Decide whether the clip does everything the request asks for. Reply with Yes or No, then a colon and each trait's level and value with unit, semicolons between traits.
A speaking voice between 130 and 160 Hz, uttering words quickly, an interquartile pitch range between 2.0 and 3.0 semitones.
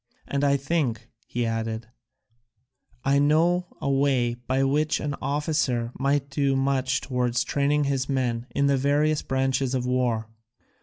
No: low, 135 Hz; average, 145 wpm; narrow, 2.4 semitones